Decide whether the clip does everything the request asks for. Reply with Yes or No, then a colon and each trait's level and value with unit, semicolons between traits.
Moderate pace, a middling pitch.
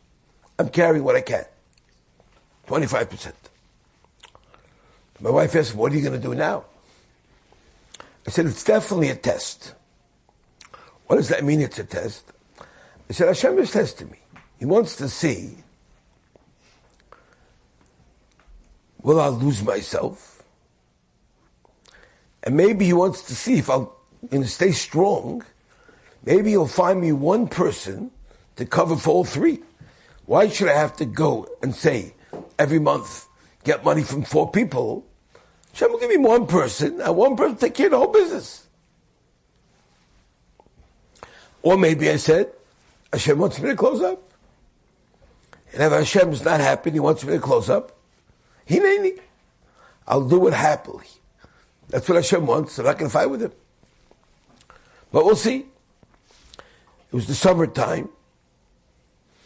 Yes: average, 145 wpm; medium, 165 Hz